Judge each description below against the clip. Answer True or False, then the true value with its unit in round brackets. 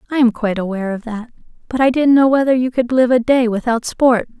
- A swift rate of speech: True (245 wpm)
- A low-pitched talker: False (245 Hz)